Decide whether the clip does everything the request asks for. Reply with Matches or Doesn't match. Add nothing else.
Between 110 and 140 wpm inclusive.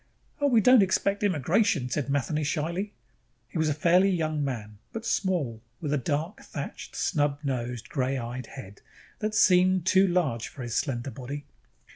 Doesn't match